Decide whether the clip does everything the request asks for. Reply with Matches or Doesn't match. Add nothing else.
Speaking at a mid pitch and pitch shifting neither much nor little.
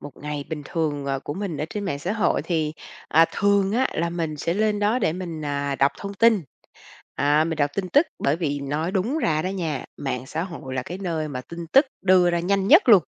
Matches